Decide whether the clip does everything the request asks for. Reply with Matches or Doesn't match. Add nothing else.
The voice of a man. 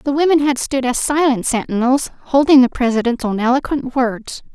Doesn't match